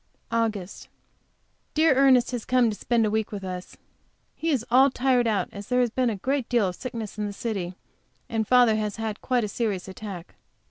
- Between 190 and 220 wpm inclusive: Yes, average, 200 wpm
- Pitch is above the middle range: Yes, high, 225 Hz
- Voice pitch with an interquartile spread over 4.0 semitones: No, average, 3.4 semitones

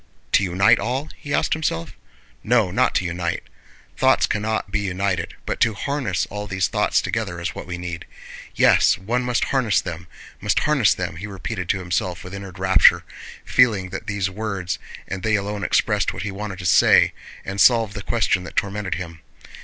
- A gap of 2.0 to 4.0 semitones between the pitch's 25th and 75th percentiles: Yes, average, 3.2 semitones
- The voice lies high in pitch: No, low, 100 Hz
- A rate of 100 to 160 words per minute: No, average, 185 wpm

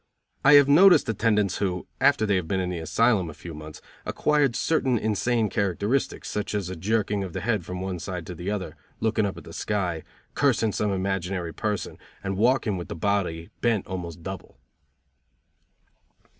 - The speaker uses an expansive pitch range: No, average, 3.8 semitones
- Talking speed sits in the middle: Yes, average, 180 wpm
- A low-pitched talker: Yes, low, 100 Hz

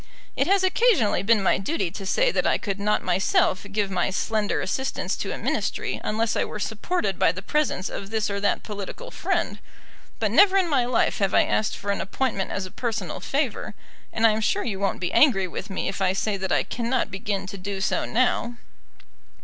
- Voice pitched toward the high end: Yes, high, 210 Hz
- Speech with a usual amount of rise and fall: Yes, average, 3.7 semitones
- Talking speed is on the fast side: Yes, fast, 215 wpm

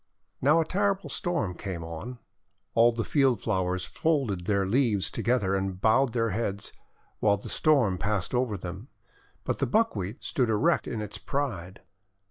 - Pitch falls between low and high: No, low, 110 Hz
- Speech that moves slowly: No, average, 155 wpm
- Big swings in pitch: Yes, wide, 5.7 semitones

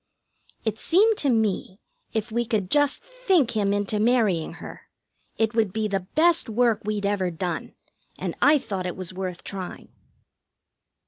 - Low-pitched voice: No, high, 215 Hz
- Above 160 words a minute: No, average, 155 wpm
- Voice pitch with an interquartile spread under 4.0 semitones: No, average, 4.4 semitones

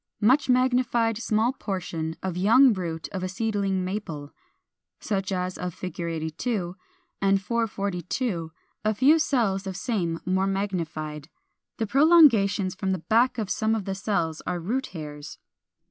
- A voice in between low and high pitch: No, high, 195 Hz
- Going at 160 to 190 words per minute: No, average, 145 wpm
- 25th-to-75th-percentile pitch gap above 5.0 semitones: No, average, 4.2 semitones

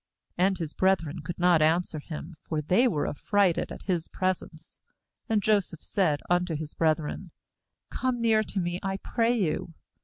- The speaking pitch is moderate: Yes, medium, 180 Hz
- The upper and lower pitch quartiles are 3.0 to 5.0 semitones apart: Yes, average, 3.6 semitones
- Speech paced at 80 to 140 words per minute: No, average, 165 wpm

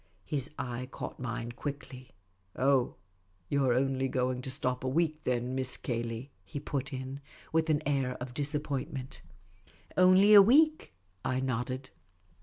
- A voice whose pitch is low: Yes, low, 130 Hz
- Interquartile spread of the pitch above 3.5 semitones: No, narrow, 2.5 semitones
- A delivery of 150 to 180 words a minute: Yes, average, 165 wpm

